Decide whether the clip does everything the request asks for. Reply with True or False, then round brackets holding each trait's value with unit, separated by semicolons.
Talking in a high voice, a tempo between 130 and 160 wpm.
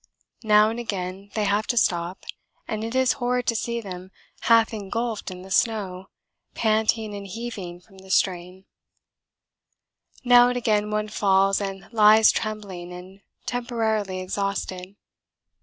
True (210 Hz; 140 wpm)